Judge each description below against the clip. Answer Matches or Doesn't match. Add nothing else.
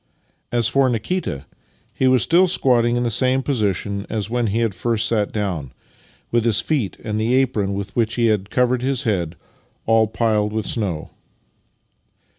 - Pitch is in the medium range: Doesn't match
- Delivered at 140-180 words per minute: Matches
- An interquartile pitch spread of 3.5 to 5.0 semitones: Doesn't match